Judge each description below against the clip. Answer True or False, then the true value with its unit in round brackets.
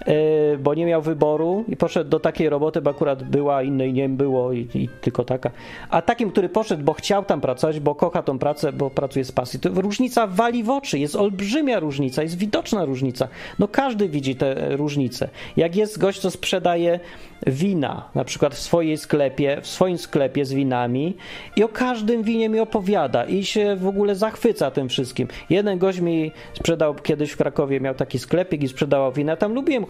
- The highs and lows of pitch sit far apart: True (6.3 semitones)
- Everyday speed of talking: False (195 wpm)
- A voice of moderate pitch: True (160 Hz)